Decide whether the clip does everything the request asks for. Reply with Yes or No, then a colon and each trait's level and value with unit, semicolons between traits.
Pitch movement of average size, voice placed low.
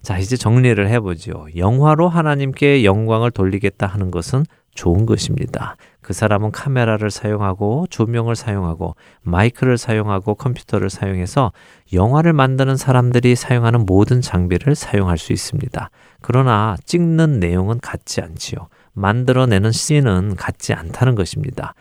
Yes: average, 4.7 semitones; low, 110 Hz